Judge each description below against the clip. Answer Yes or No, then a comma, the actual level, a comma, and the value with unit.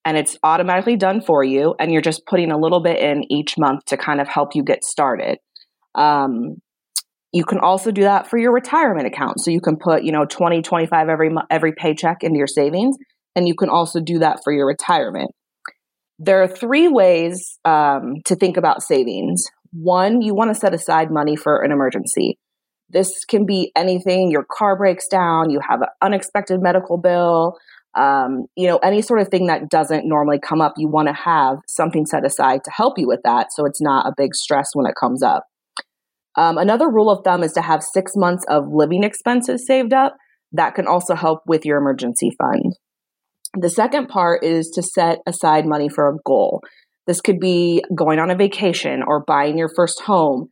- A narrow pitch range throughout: No, average, 3.7 semitones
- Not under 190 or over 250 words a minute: Yes, average, 200 wpm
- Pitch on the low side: No, medium, 170 Hz